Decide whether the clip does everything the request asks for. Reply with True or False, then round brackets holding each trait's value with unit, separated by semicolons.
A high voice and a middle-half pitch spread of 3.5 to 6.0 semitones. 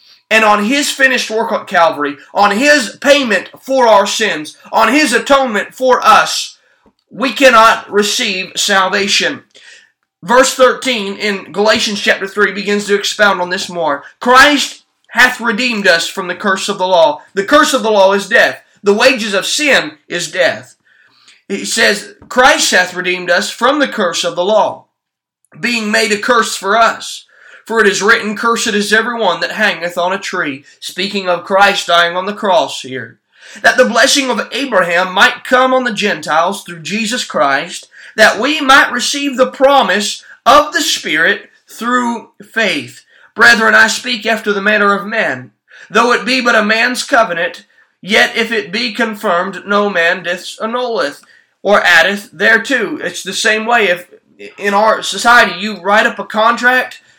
True (215 Hz; 4.2 semitones)